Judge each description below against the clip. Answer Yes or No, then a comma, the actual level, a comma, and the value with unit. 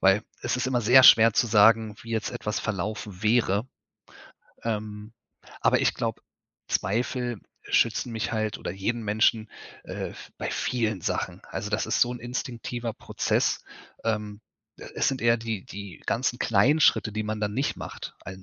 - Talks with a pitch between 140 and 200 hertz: No, low, 110 Hz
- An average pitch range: No, narrow, 2.3 semitones